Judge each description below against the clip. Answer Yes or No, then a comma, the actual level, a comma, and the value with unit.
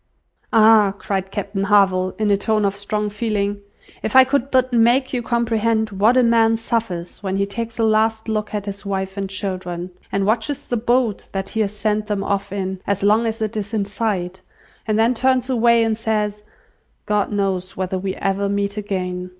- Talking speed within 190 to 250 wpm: Yes, average, 195 wpm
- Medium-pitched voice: No, high, 210 Hz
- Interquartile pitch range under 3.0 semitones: Yes, narrow, 2.4 semitones